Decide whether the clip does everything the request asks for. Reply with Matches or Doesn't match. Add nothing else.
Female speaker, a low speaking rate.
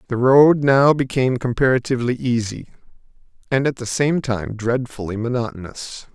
Doesn't match